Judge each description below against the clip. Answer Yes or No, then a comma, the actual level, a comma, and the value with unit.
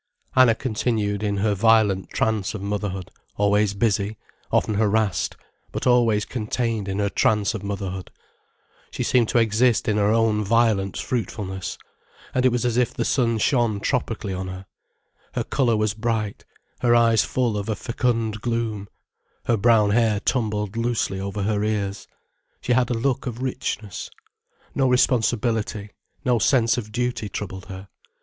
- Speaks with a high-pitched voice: No, low, 110 Hz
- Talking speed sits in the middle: Yes, average, 155 wpm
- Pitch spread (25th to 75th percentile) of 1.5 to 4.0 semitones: Yes, narrow, 2.6 semitones